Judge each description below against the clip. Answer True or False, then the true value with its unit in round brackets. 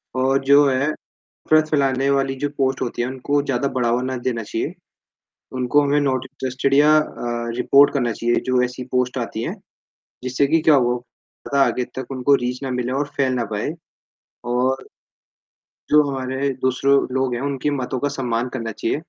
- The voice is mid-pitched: False (130 Hz)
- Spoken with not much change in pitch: True (2.0 semitones)